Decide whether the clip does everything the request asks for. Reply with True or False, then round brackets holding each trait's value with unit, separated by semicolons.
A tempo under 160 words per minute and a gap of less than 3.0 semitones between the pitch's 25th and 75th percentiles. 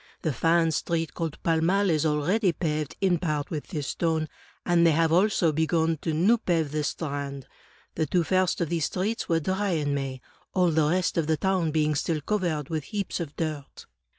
False (200 wpm; 2.6 semitones)